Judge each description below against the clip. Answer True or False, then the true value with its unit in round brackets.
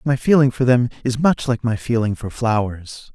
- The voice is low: True (120 Hz)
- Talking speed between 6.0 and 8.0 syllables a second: False (4.9 syllables/s)